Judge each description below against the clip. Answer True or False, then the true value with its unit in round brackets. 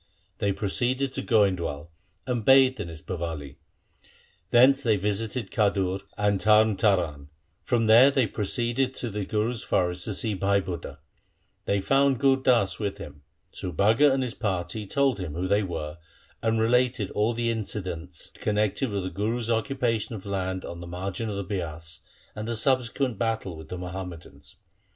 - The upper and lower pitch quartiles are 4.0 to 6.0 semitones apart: True (4.3 semitones)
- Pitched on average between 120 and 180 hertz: False (105 Hz)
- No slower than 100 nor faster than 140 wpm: False (165 wpm)